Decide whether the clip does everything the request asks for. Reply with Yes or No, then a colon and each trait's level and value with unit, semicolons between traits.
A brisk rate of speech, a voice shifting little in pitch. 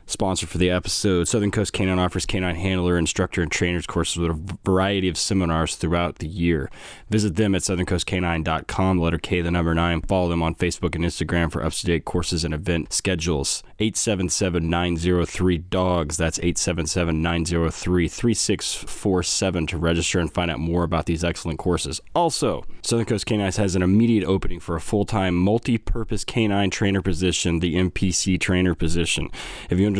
No: average, 180 wpm; narrow, 2.1 semitones